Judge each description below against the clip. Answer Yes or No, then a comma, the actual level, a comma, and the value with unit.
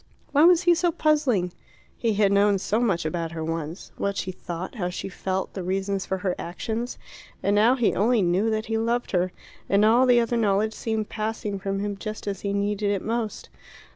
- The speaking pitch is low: No, high, 205 Hz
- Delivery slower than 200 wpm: No, fast, 205 wpm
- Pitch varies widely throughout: No, average, 3.1 semitones